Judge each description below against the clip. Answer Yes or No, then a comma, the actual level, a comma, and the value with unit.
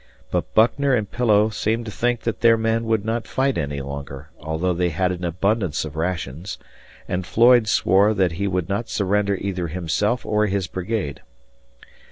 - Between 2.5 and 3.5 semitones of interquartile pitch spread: No, average, 4.5 semitones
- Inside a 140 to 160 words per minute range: No, average, 175 wpm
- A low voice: Yes, low, 100 Hz